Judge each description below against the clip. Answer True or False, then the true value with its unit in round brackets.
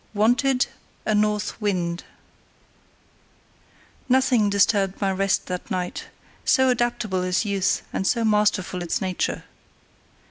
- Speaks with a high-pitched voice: True (205 Hz)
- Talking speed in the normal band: False (110 wpm)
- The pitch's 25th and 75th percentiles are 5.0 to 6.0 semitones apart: False (3.3 semitones)